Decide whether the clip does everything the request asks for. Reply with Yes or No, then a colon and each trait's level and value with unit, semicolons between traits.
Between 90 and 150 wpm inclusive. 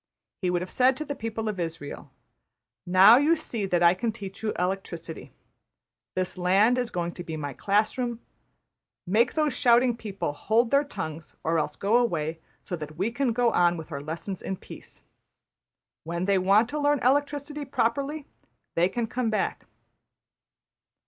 No: average, 170 wpm